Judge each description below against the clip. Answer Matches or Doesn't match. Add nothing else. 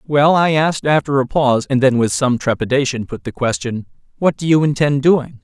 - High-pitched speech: Doesn't match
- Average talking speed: Doesn't match